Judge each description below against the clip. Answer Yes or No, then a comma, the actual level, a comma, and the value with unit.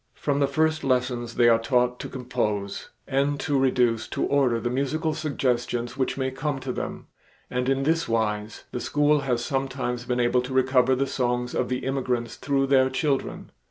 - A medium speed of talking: Yes, average, 185 wpm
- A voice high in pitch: No, low, 130 Hz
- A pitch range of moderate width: No, narrow, 2.1 semitones